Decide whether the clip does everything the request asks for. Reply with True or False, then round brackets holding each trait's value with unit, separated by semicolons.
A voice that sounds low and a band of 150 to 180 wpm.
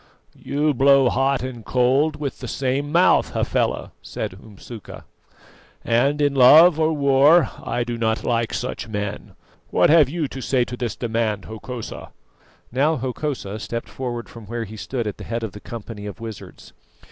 True (125 Hz; 170 wpm)